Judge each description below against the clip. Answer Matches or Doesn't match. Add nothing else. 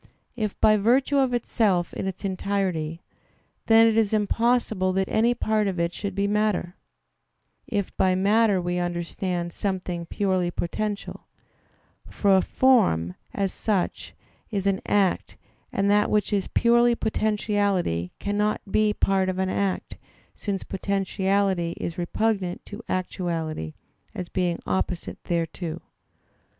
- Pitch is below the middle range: Doesn't match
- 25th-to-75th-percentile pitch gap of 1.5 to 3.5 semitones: Matches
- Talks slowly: Matches